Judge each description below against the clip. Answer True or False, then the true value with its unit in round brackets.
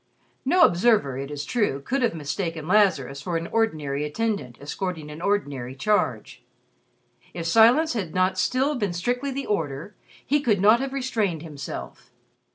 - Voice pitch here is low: False (185 Hz)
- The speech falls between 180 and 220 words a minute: False (155 wpm)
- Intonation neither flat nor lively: False (7.6 semitones)